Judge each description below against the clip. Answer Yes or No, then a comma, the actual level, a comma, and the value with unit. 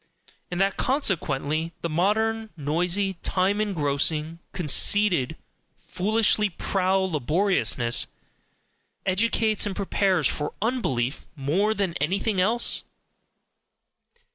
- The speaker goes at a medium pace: No, slow, 90 wpm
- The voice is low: No, medium, 185 Hz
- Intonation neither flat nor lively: Yes, average, 4.9 semitones